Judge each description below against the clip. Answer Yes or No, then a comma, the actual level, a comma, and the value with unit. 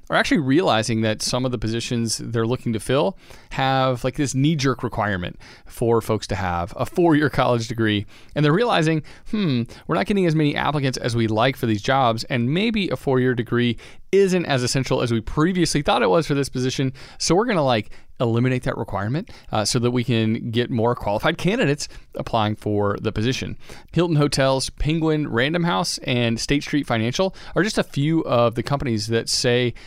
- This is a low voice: Yes, low, 125 Hz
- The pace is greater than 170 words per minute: Yes, average, 200 wpm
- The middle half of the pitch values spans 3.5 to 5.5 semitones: Yes, average, 4.2 semitones